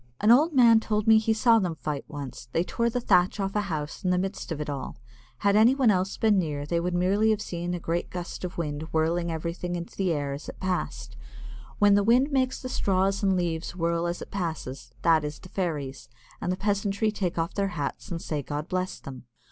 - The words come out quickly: Yes, fast, 220 wpm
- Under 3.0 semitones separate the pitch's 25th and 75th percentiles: No, average, 4.2 semitones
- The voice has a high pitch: No, medium, 180 Hz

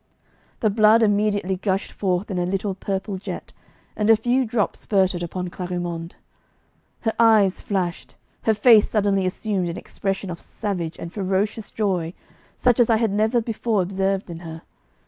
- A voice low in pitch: No, high, 195 Hz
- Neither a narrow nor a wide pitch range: Yes, average, 3.0 semitones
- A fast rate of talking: No, average, 160 wpm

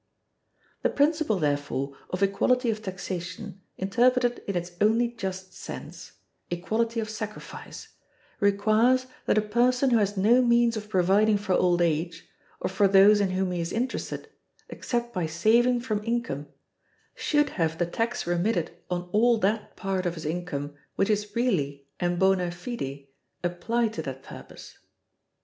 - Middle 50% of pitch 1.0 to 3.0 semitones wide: No, average, 4.8 semitones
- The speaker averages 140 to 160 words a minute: Yes, average, 150 wpm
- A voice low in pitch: No, high, 200 Hz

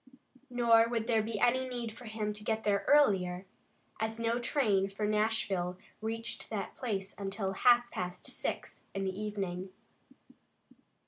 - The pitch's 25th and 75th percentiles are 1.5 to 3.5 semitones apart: Yes, average, 2.9 semitones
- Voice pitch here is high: Yes, high, 215 Hz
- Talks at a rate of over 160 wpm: No, average, 145 wpm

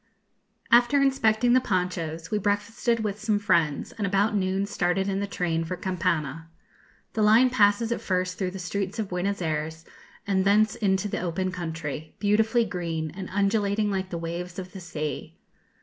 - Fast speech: No, average, 170 wpm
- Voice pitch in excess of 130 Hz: Yes, high, 190 Hz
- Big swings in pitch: No, average, 3.3 semitones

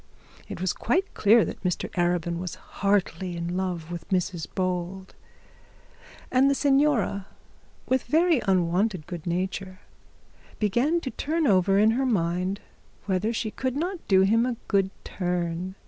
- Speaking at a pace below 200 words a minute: Yes, average, 145 wpm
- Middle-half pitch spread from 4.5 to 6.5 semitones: Yes, average, 5.0 semitones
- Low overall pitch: No, high, 190 Hz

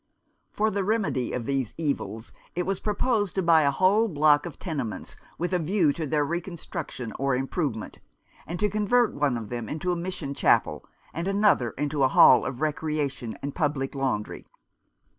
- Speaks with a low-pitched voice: No, medium, 155 Hz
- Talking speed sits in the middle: Yes, average, 175 wpm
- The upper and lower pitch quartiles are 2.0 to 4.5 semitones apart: No, wide, 5.5 semitones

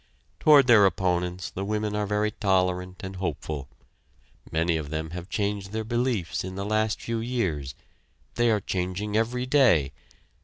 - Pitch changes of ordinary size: Yes, average, 3.6 semitones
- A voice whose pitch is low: Yes, low, 100 Hz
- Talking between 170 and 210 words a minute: No, average, 155 wpm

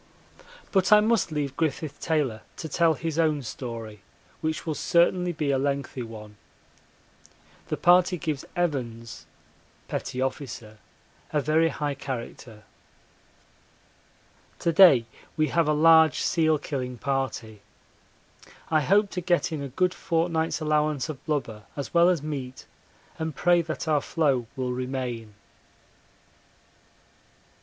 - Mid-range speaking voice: Yes, medium, 150 Hz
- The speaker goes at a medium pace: No, slow, 125 wpm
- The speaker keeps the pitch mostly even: No, average, 4.1 semitones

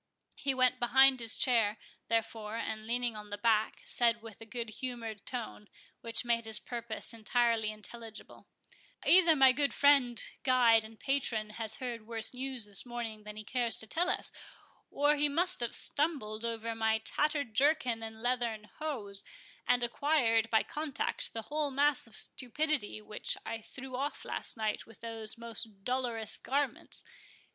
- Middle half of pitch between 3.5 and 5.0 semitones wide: No, average, 3.1 semitones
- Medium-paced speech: Yes, average, 160 wpm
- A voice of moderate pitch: No, high, 235 Hz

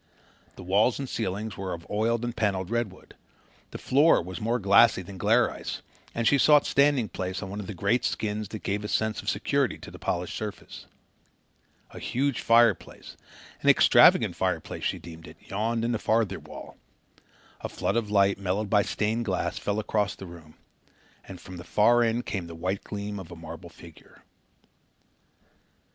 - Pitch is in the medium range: No, low, 105 Hz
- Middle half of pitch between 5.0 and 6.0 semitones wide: No, average, 3.7 semitones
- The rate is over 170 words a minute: Yes, average, 180 wpm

